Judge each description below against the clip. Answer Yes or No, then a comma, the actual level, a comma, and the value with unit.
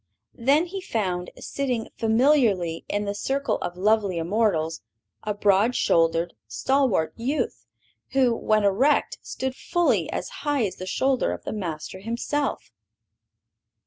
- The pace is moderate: No, slow, 130 wpm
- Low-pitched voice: No, high, 220 Hz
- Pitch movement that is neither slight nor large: No, wide, 6.3 semitones